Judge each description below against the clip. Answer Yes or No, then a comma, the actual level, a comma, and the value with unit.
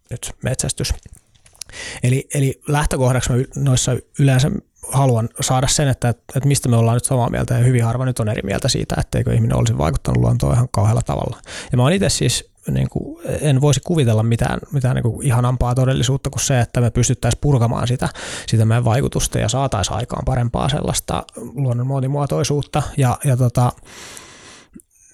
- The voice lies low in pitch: Yes, low, 125 Hz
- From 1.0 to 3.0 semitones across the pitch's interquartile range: Yes, narrow, 2.6 semitones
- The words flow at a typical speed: No, fast, 165 wpm